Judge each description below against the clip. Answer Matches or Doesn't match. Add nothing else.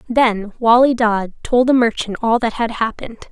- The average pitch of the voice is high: Matches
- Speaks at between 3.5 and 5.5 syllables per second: Matches